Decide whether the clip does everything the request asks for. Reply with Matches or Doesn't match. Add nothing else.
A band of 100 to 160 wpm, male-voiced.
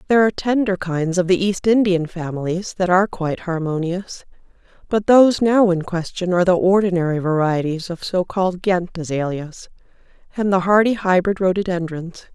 Doesn't match